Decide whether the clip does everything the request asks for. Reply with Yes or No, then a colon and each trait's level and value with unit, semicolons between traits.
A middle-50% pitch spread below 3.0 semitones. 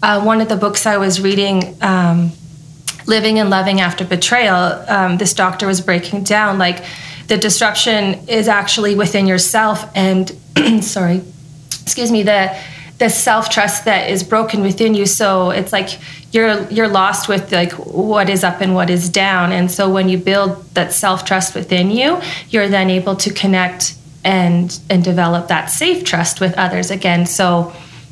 Yes: narrow, 2.6 semitones